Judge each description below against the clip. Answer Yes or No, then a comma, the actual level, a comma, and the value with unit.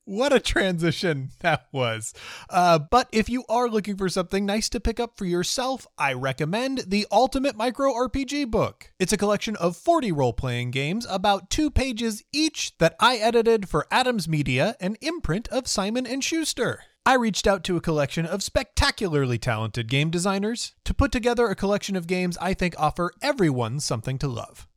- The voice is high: Yes, high, 200 Hz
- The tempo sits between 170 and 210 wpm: Yes, average, 175 wpm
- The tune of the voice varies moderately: No, wide, 6.9 semitones